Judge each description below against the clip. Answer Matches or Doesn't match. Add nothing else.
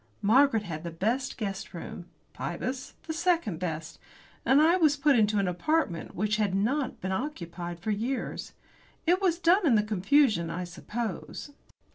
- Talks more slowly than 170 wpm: Matches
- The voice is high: Matches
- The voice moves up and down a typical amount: Doesn't match